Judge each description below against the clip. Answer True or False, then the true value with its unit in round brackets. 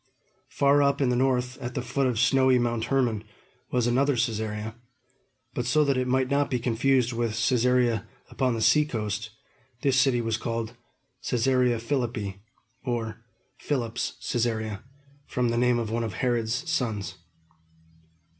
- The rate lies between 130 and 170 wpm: True (145 wpm)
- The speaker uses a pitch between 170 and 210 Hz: False (120 Hz)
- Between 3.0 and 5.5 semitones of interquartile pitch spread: False (2.4 semitones)